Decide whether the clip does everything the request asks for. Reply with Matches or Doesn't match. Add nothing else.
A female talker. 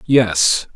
Doesn't match